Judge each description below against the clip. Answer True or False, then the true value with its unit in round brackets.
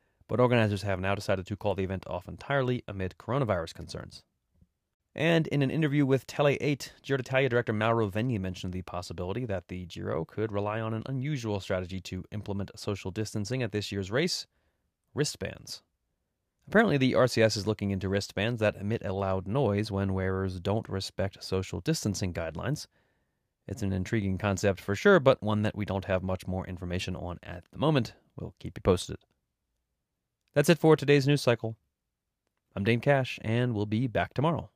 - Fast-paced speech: False (175 wpm)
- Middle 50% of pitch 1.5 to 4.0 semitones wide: False (4.7 semitones)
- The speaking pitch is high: False (105 Hz)